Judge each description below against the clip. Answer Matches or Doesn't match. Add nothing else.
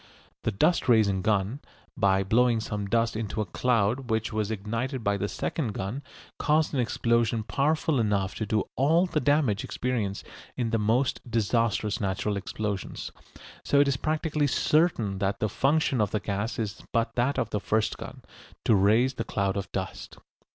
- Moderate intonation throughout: Matches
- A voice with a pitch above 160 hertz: Doesn't match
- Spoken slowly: Doesn't match